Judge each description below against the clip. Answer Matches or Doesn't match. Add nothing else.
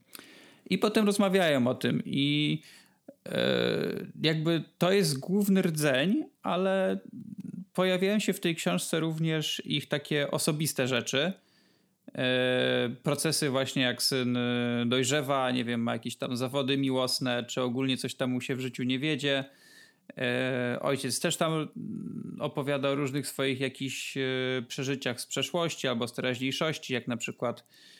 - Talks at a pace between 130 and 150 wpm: Matches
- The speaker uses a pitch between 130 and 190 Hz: Matches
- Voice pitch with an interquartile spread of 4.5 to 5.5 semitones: Matches